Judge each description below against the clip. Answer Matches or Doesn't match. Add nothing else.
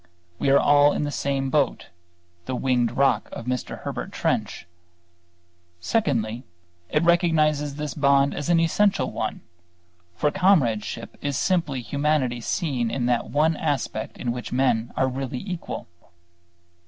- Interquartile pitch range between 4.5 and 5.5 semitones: Doesn't match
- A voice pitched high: Doesn't match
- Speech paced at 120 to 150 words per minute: Matches